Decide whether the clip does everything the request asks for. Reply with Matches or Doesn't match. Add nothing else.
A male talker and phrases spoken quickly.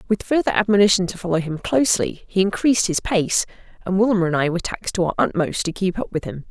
Doesn't match